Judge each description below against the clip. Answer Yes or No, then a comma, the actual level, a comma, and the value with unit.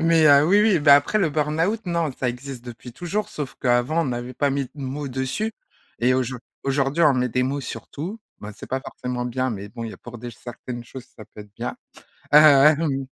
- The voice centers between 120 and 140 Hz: Yes, low, 135 Hz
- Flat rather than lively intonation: No, average, 3.9 semitones